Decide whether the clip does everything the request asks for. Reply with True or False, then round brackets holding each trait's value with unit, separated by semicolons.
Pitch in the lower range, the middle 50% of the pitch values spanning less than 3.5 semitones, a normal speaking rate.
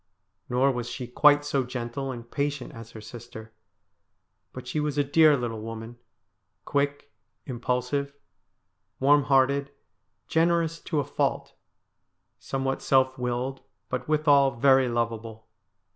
False (130 Hz; 2.9 semitones; 130 wpm)